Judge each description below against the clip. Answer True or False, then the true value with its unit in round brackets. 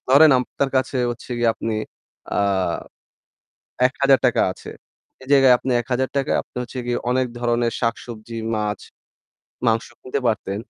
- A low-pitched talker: True (125 Hz)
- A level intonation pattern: True (2.2 semitones)